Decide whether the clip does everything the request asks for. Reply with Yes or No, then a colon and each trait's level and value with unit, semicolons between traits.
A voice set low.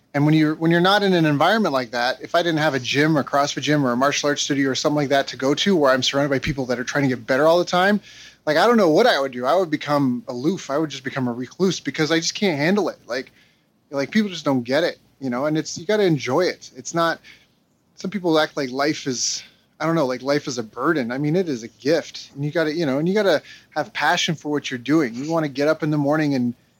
No: medium, 150 Hz